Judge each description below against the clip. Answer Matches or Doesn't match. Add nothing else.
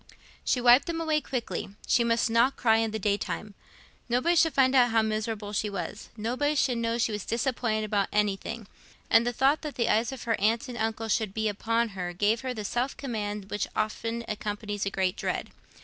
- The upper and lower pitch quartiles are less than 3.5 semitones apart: Matches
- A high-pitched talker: Matches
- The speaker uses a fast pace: Matches